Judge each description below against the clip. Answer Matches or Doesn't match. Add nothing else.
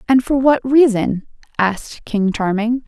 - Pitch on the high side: Matches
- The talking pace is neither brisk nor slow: Matches